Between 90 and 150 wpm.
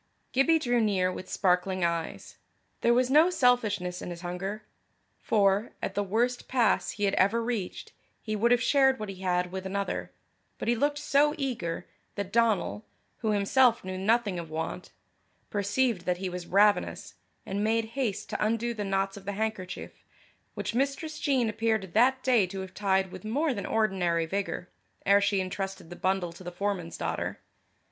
No: average, 175 wpm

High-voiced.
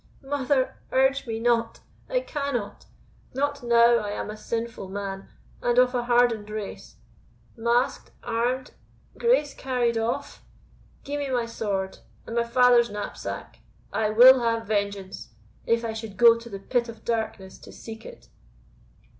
Yes: high, 235 Hz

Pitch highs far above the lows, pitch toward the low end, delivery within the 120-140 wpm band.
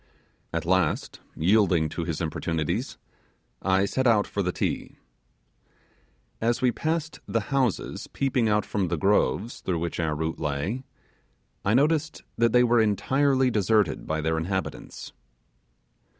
Yes: wide, 6.4 semitones; low, 100 Hz; slow, 135 wpm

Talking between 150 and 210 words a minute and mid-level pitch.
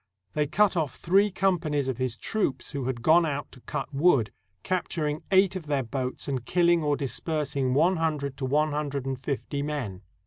Yes: average, 185 wpm; medium, 145 Hz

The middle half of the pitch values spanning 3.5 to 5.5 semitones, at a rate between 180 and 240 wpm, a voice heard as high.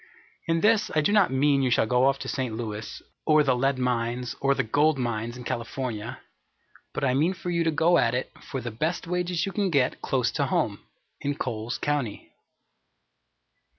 No: average, 4.8 semitones; average, 195 wpm; low, 135 Hz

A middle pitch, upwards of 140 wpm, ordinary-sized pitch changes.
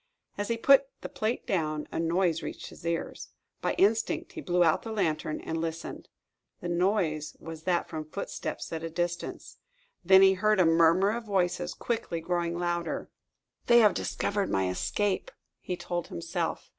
Yes: medium, 175 Hz; average, 170 wpm; average, 3.8 semitones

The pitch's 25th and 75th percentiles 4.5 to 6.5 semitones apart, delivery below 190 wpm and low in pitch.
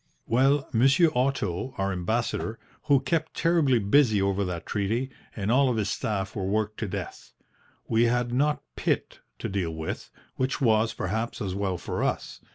Yes: average, 4.8 semitones; average, 165 wpm; low, 110 Hz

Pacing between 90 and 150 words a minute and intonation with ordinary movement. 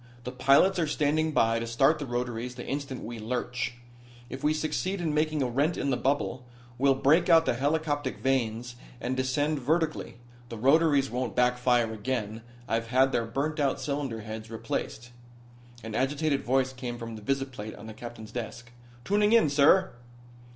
No: average, 170 wpm; average, 3.8 semitones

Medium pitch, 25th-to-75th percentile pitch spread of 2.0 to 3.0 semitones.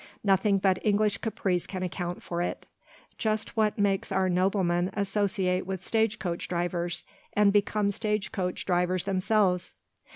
No: high, 195 Hz; narrow, 2.4 semitones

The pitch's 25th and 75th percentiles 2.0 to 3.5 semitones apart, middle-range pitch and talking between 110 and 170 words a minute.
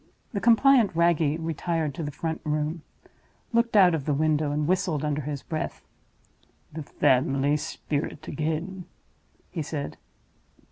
Yes: average, 2.7 semitones; medium, 155 Hz; slow, 135 wpm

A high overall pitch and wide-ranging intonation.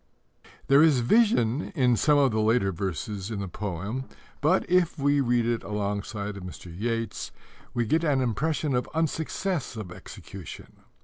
No: low, 120 Hz; wide, 6.1 semitones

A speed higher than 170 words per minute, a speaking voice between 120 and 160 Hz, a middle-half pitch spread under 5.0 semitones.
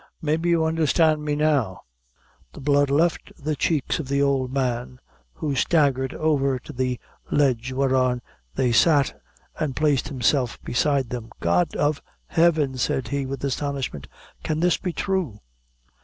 No: average, 145 wpm; medium, 140 Hz; average, 3.1 semitones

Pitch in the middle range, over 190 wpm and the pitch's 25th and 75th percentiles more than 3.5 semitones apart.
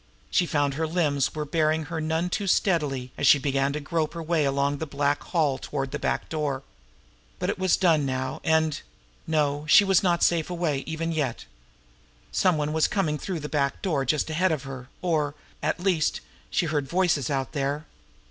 No: medium, 155 Hz; average, 200 wpm; average, 2.9 semitones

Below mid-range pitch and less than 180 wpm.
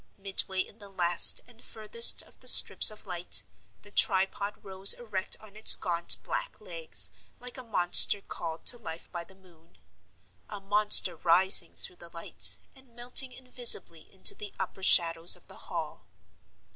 No: high, 195 Hz; average, 160 wpm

